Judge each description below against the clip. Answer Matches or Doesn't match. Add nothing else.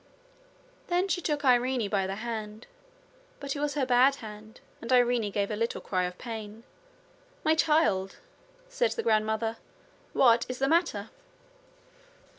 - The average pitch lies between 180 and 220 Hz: Doesn't match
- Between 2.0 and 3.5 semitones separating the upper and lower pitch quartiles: Doesn't match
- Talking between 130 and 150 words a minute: Matches